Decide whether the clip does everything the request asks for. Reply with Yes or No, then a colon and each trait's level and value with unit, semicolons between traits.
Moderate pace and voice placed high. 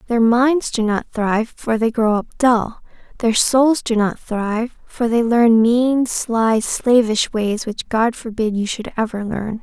Yes: average, 180 wpm; high, 230 Hz